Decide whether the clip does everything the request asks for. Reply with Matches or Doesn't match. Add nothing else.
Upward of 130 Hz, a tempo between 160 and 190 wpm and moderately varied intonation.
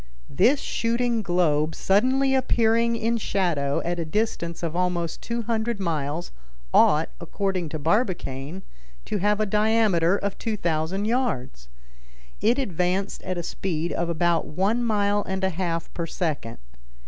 Doesn't match